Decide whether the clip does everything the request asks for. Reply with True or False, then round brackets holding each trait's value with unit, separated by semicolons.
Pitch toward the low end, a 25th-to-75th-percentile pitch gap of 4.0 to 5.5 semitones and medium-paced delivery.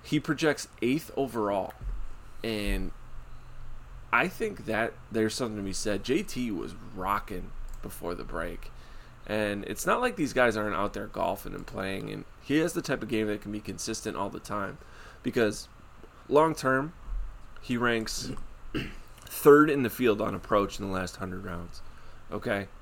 True (110 Hz; 4.4 semitones; 165 wpm)